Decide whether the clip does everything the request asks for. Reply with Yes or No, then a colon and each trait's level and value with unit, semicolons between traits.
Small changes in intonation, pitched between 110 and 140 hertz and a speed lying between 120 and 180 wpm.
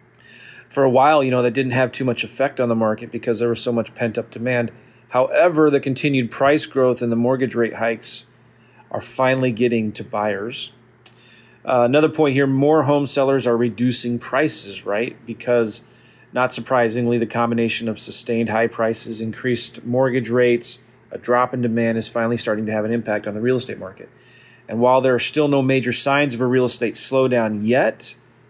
No: narrow, 2.0 semitones; low, 120 Hz; average, 190 wpm